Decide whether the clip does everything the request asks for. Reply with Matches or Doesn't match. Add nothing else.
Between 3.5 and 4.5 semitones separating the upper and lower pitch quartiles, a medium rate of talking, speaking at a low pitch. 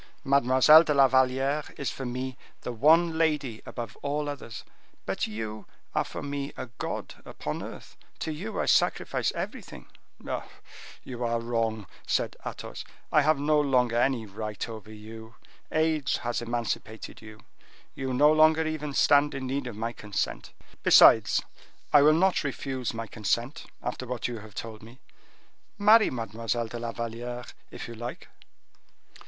Matches